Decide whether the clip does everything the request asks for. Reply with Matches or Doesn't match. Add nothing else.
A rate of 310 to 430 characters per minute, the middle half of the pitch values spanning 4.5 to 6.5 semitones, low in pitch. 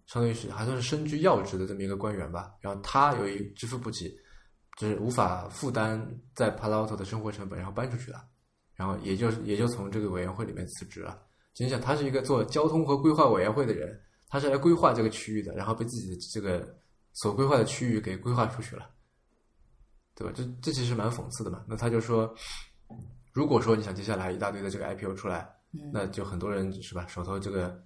Doesn't match